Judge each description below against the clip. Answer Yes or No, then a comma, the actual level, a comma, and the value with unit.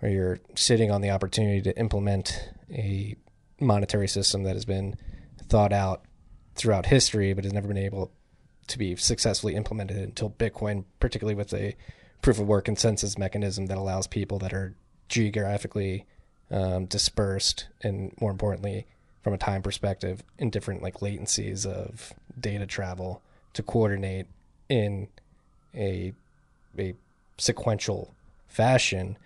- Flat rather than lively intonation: Yes, narrow, 1.9 semitones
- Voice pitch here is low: Yes, low, 100 Hz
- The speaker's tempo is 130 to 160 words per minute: Yes, slow, 135 wpm